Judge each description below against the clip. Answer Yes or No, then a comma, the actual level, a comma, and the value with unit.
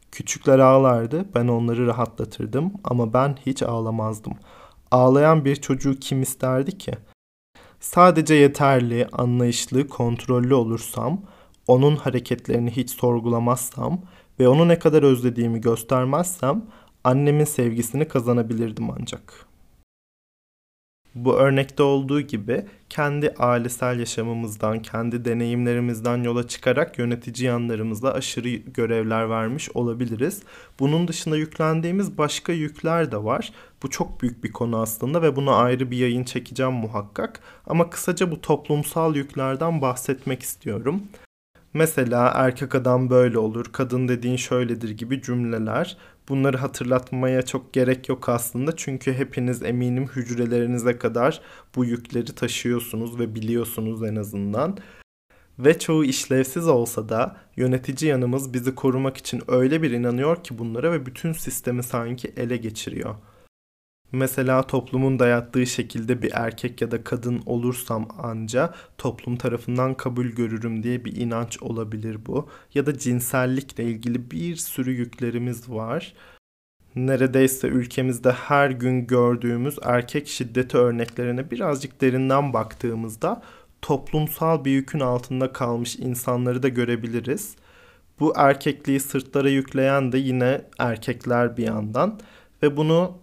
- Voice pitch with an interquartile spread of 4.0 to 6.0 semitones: No, narrow, 2.5 semitones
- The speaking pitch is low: Yes, low, 125 Hz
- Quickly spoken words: No, average, 120 wpm